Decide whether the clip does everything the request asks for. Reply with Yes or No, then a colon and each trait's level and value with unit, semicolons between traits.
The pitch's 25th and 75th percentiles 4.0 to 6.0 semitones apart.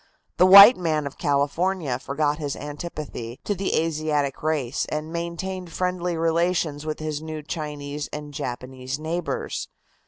No: average, 2.9 semitones